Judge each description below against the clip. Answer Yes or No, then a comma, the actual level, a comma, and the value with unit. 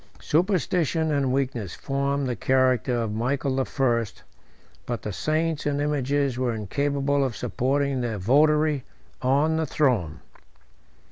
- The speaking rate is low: Yes, slow, 130 wpm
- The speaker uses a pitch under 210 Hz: Yes, low, 135 Hz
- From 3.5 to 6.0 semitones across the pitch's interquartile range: No, average, 2.9 semitones